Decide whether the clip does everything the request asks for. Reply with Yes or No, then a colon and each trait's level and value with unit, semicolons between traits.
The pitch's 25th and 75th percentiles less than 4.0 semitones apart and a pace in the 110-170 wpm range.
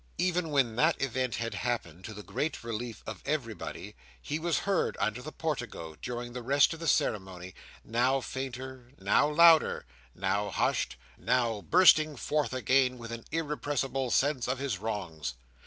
No: average, 4.6 semitones; average, 155 wpm